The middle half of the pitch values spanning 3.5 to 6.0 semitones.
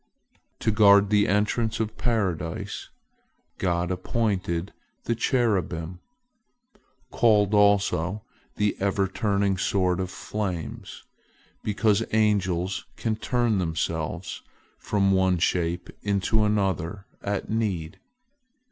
No: average, 2.8 semitones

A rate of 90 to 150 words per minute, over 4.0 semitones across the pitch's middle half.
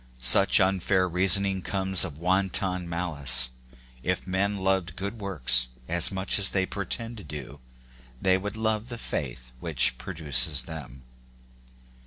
Yes: average, 140 wpm; average, 4.5 semitones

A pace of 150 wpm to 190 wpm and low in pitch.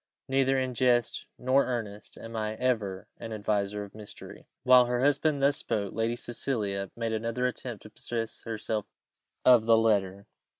Yes: average, 160 wpm; low, 115 Hz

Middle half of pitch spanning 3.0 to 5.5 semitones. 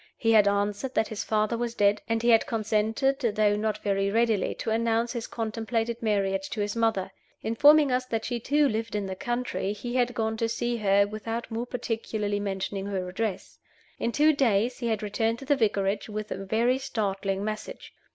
No: narrow, 2.5 semitones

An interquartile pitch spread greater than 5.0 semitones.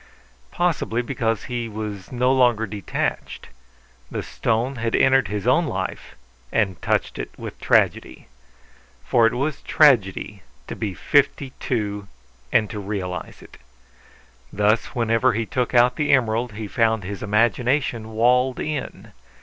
No: average, 3.3 semitones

